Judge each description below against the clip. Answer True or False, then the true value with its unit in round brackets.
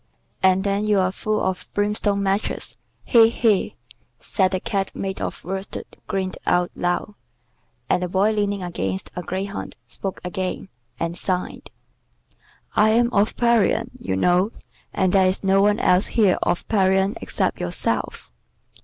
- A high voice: True (195 Hz)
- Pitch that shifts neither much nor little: False (2.0 semitones)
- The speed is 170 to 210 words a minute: False (145 wpm)